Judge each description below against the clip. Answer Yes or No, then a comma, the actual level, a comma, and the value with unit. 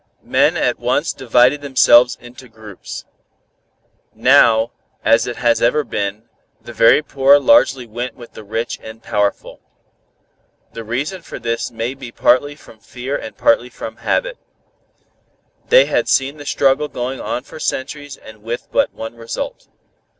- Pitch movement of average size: Yes, average, 3.5 semitones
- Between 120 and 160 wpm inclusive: Yes, average, 150 wpm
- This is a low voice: Yes, low, 120 Hz